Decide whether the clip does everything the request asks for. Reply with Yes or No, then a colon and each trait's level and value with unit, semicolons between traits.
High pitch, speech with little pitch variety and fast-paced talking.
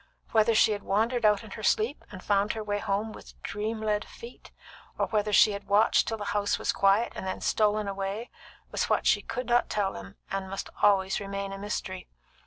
Yes: high, 205 Hz; narrow, 1.7 semitones; fast, 210 wpm